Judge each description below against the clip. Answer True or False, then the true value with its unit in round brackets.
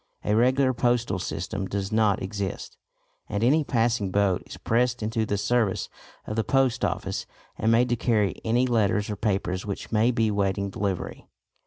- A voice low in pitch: True (110 Hz)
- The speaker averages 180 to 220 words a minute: False (170 wpm)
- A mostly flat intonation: False (3.2 semitones)